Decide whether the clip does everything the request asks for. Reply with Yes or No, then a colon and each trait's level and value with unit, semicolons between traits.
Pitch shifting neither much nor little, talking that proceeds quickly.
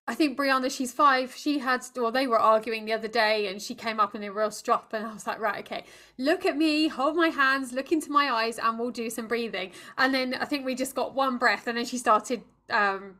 Yes: average, 3.3 semitones; fast, 260 wpm